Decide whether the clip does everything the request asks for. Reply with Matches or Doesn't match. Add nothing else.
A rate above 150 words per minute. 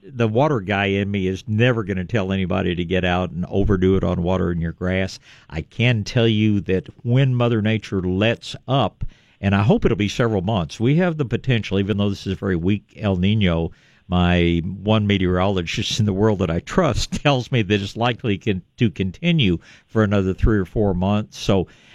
Matches